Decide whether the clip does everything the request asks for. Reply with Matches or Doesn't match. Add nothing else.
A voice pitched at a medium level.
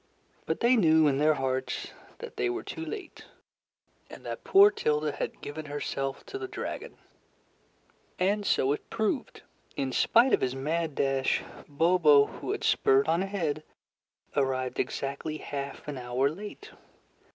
Matches